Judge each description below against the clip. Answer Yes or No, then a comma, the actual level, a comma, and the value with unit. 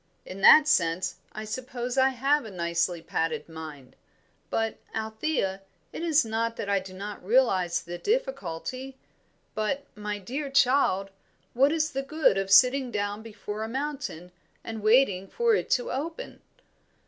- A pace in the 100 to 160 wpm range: Yes, average, 150 wpm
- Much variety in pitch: Yes, wide, 6.0 semitones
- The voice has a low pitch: No, high, 220 Hz